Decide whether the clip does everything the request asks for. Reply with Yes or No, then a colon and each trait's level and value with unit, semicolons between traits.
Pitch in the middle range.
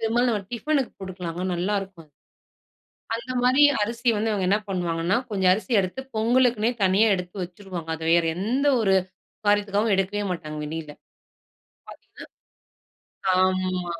No: high, 195 Hz